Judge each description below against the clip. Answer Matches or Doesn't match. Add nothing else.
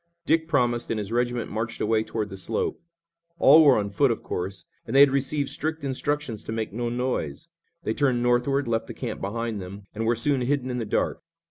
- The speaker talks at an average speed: Doesn't match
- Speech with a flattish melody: Doesn't match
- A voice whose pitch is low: Matches